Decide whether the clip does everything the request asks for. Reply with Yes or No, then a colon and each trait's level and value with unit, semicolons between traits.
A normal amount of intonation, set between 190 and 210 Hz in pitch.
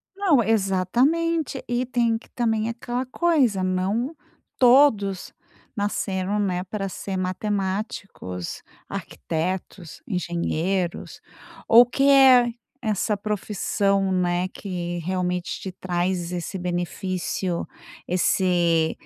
Yes: average, 4.6 semitones; high, 195 Hz